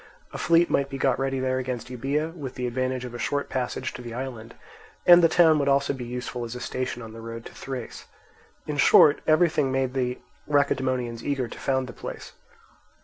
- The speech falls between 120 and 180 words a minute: No, fast, 205 wpm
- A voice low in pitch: Yes, low, 130 Hz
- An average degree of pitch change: No, narrow, 2.3 semitones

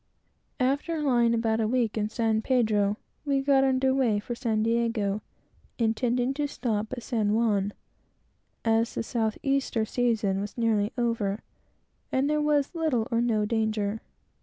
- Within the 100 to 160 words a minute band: Yes, average, 150 wpm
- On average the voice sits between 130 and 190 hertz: No, high, 230 Hz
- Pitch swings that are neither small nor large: Yes, average, 3.1 semitones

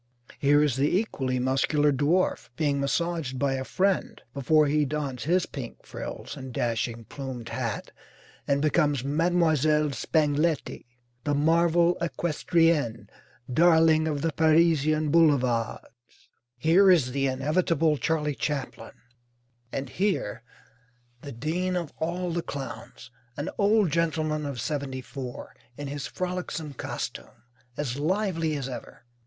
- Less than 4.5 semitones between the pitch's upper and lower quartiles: Yes, average, 3.6 semitones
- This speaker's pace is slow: Yes, slow, 125 wpm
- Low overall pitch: No, medium, 150 Hz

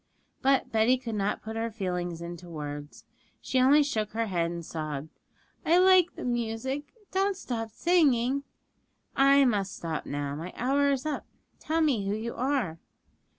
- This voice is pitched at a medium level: No, high, 230 Hz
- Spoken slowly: No, average, 160 wpm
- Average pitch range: No, wide, 7.7 semitones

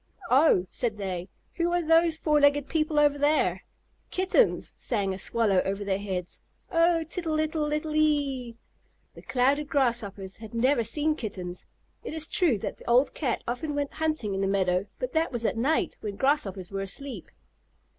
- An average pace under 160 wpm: No, average, 175 wpm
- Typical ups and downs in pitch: No, wide, 7.3 semitones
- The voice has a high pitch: Yes, very high, 270 Hz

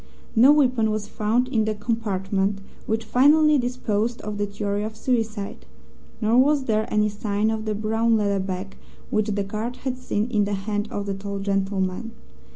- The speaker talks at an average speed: Yes, average, 175 wpm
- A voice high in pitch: Yes, high, 215 Hz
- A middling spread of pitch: No, narrow, 2.3 semitones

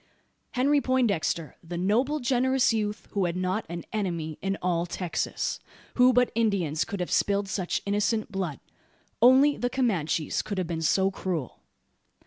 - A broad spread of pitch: Yes, wide, 5.7 semitones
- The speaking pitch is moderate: No, high, 200 Hz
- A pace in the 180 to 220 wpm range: No, average, 150 wpm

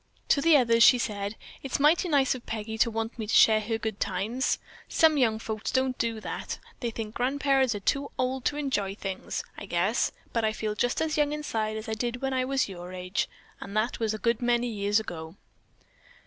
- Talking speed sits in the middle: No, fast, 215 wpm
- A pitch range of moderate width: Yes, average, 3.6 semitones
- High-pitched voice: Yes, high, 230 Hz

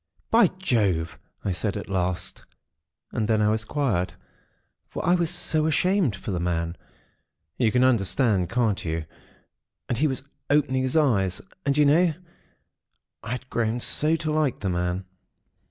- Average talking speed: Yes, average, 155 wpm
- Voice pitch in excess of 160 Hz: No, low, 115 Hz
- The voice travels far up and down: Yes, wide, 7.9 semitones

